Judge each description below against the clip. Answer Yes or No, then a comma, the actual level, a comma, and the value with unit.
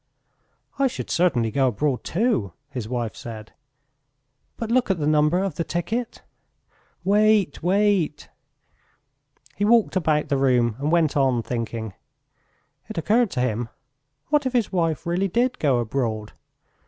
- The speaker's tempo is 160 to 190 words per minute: No, average, 140 wpm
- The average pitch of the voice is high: No, medium, 155 Hz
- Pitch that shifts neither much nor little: No, wide, 8.6 semitones